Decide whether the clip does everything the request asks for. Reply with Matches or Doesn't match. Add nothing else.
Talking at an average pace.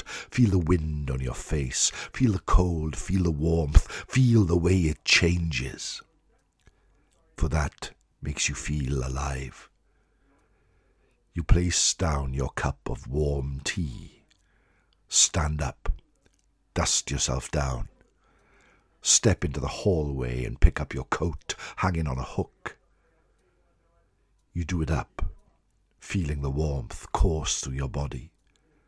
Doesn't match